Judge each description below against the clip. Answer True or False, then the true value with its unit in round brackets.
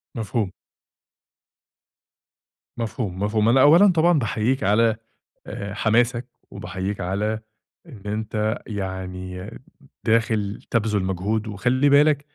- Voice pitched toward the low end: True (110 Hz)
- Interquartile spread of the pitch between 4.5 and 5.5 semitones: False (3.3 semitones)